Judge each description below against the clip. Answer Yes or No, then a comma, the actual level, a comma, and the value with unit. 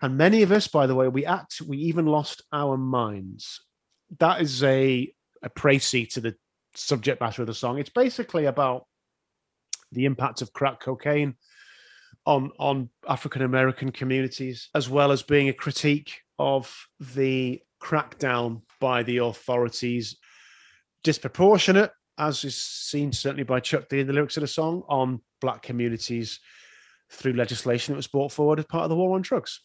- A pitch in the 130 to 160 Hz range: Yes, low, 135 Hz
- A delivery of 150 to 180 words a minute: Yes, average, 165 wpm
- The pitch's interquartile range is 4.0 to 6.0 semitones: No, average, 3.1 semitones